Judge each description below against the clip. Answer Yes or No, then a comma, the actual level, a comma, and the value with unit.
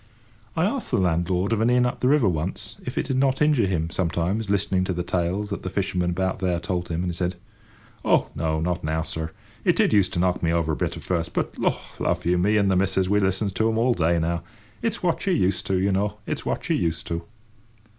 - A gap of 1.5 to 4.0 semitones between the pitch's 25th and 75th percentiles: Yes, average, 3.3 semitones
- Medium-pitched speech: No, very low, 95 Hz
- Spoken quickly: Yes, fast, 250 wpm